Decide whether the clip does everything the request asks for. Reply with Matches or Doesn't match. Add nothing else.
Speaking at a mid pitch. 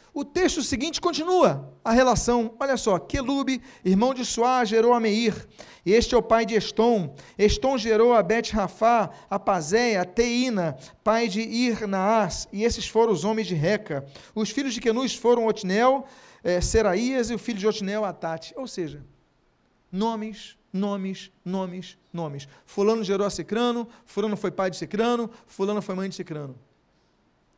Doesn't match